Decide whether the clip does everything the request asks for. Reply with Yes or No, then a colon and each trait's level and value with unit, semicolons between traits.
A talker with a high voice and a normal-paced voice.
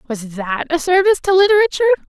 Yes: very high, 335 Hz; average, 170 wpm